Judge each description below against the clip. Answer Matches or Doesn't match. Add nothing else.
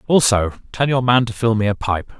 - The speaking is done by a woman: Doesn't match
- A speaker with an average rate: Doesn't match